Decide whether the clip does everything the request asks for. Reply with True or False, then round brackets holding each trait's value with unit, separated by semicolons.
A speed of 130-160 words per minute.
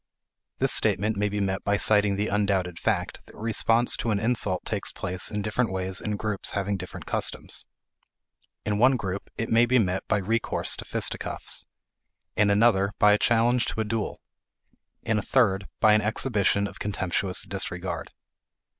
False (170 wpm)